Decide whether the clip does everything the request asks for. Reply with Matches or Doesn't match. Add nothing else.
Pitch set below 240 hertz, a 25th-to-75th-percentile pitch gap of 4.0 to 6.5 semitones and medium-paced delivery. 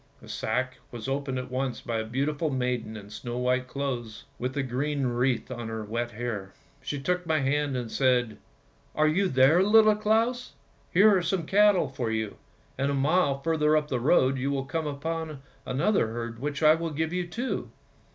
Matches